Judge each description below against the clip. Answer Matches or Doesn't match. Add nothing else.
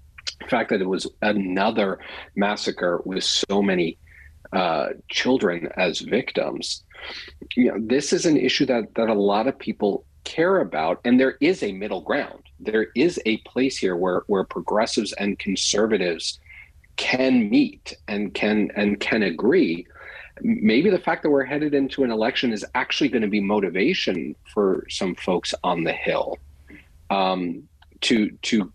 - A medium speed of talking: Matches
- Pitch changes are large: Matches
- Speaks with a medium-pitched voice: Doesn't match